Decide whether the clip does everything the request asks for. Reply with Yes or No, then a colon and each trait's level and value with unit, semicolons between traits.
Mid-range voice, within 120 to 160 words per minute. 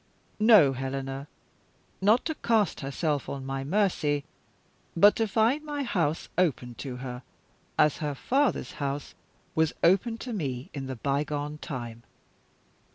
Yes: medium, 150 Hz; slow, 135 wpm